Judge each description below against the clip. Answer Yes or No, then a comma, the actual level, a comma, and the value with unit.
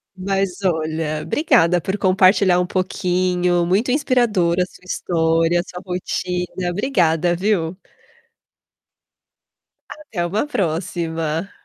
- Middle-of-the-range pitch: Yes, medium, 180 Hz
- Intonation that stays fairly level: Yes, narrow, 2.3 semitones